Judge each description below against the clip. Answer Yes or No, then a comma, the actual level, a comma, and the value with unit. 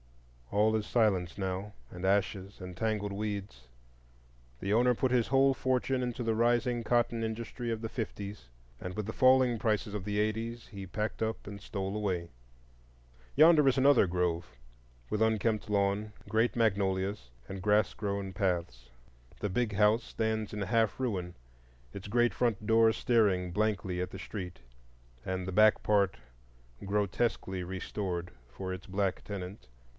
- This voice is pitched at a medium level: No, low, 105 Hz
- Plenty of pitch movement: No, average, 3.0 semitones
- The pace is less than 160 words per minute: Yes, average, 150 wpm